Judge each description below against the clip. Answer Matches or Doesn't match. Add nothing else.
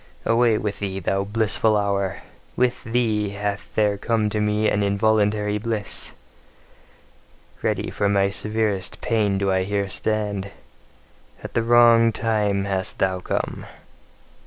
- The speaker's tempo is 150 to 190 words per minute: Doesn't match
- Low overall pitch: Matches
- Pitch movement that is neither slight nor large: Doesn't match